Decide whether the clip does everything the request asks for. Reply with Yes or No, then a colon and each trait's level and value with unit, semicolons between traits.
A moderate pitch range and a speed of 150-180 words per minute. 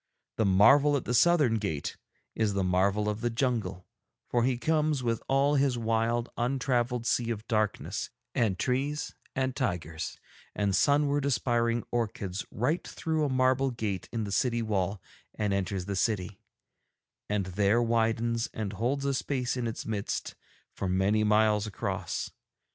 Yes: average, 4.0 semitones; average, 155 wpm